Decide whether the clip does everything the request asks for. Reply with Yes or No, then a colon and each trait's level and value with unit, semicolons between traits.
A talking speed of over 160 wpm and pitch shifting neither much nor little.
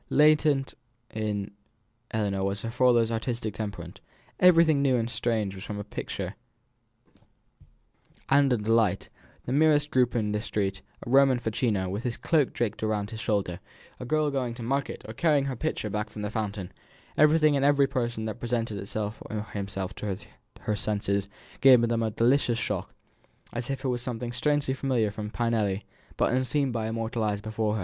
Yes: average, 170 wpm; average, 3.9 semitones